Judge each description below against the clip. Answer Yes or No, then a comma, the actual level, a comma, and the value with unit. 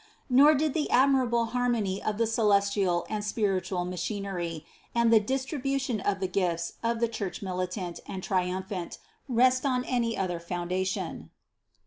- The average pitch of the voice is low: No, high, 205 Hz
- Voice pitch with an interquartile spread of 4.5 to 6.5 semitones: Yes, average, 4.8 semitones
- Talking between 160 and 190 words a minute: No, average, 140 wpm